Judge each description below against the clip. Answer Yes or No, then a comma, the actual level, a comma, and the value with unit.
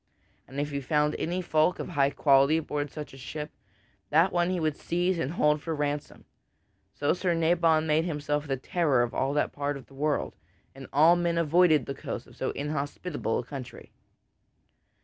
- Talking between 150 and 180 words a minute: No, average, 190 wpm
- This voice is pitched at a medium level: Yes, medium, 150 Hz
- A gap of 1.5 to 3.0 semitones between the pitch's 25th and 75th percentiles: Yes, average, 2.7 semitones